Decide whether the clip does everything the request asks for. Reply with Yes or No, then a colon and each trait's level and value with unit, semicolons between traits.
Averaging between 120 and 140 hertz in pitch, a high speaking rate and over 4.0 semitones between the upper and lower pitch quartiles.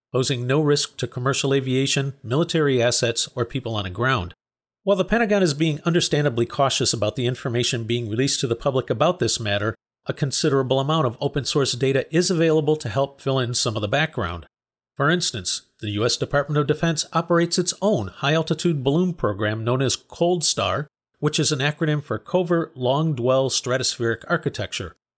No: low, 135 Hz; average, 180 wpm; average, 4.5 semitones